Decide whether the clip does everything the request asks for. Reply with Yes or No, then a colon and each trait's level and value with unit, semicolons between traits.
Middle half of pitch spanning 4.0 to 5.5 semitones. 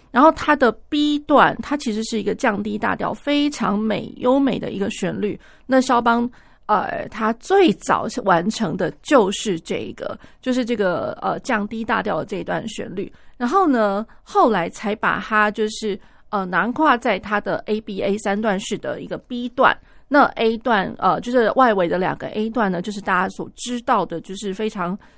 No: average, 3.6 semitones